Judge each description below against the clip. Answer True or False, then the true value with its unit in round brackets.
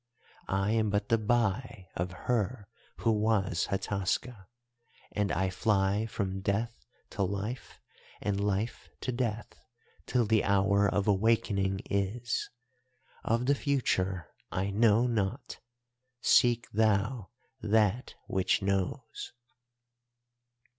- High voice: False (105 Hz)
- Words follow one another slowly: True (110 wpm)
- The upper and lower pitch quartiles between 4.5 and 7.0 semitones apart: False (3.0 semitones)